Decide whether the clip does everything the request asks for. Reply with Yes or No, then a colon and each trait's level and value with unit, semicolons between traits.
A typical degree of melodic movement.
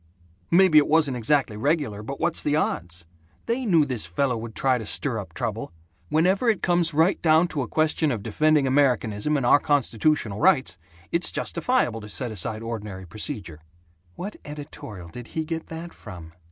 No: wide, 6.7 semitones